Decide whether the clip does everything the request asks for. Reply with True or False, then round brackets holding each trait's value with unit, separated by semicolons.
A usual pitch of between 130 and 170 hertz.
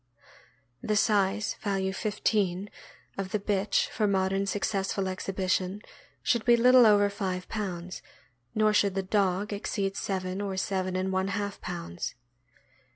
False (195 Hz)